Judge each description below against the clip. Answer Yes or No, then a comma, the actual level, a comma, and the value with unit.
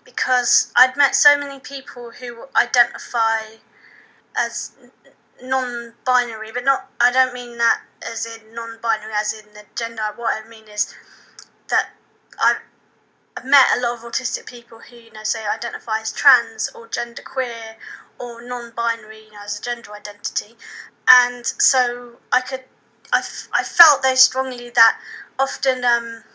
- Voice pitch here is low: No, high, 240 Hz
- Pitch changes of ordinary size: No, narrow, 2.1 semitones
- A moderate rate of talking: Yes, average, 150 wpm